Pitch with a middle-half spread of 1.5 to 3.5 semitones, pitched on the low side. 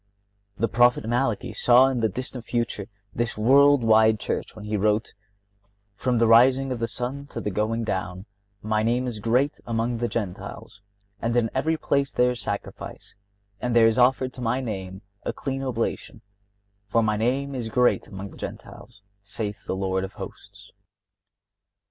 Yes: average, 2.9 semitones; low, 115 Hz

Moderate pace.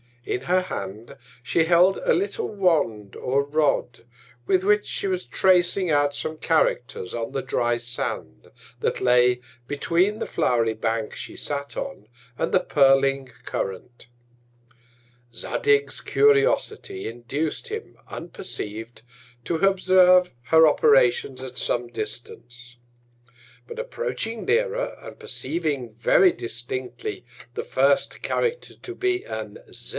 No: slow, 120 wpm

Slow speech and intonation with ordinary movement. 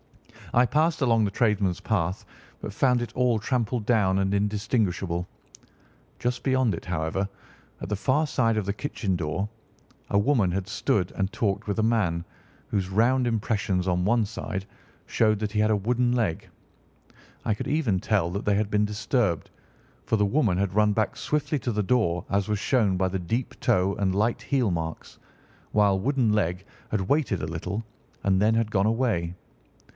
No: average, 180 wpm; average, 3.6 semitones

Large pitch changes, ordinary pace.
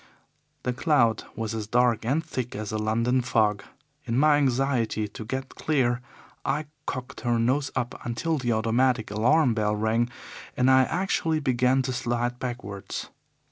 No: average, 2.8 semitones; average, 155 wpm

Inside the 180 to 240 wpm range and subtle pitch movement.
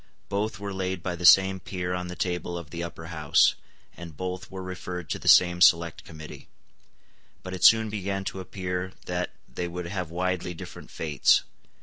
Yes: average, 185 wpm; narrow, 1.5 semitones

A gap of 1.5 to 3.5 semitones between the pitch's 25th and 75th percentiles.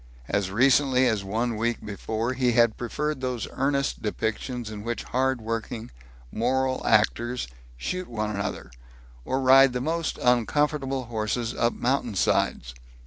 Yes: average, 3.1 semitones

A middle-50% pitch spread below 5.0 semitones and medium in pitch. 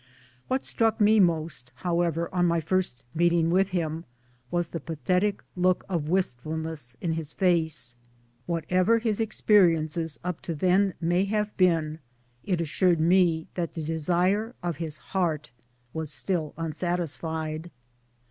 Yes: narrow, 2.5 semitones; medium, 170 Hz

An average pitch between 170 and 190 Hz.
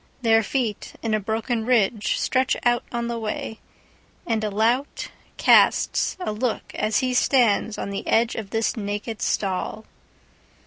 No: high, 225 Hz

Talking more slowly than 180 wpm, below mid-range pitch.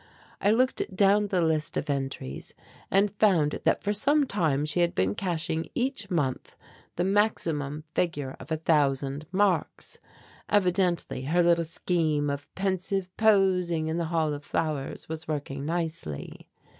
No: average, 145 wpm; medium, 170 Hz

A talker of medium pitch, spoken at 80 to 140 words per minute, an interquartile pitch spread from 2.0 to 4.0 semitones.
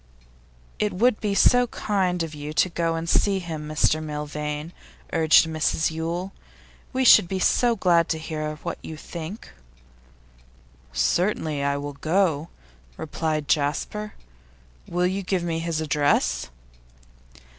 Yes: medium, 165 Hz; slow, 135 wpm; average, 3.3 semitones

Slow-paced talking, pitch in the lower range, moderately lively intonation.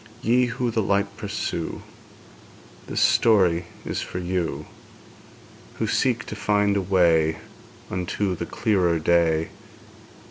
Yes: slow, 115 wpm; low, 100 Hz; average, 3.8 semitones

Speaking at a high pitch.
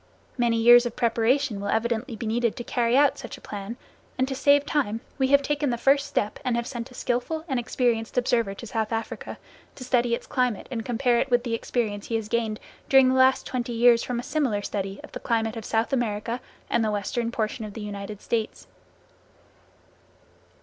Yes: high, 235 Hz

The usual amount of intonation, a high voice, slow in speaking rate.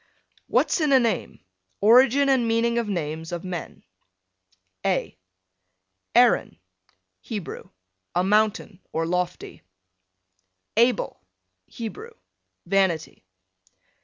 Yes: average, 4.9 semitones; high, 210 Hz; slow, 90 wpm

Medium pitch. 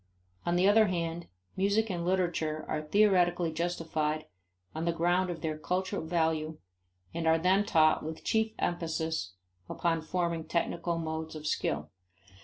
Yes: medium, 170 Hz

